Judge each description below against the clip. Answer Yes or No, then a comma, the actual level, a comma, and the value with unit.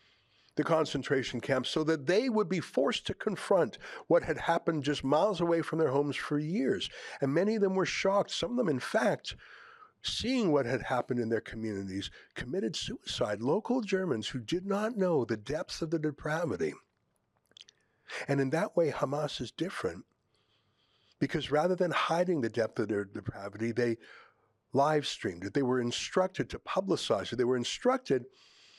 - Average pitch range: No, wide, 6.4 semitones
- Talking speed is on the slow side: No, average, 170 wpm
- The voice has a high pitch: No, medium, 150 Hz